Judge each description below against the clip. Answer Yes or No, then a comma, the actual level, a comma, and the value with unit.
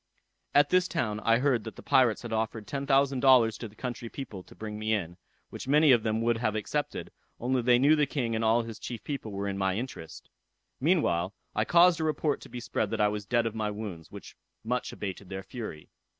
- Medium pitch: No, low, 115 Hz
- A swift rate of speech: Yes, fast, 230 wpm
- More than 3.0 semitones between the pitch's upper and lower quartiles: Yes, average, 4.1 semitones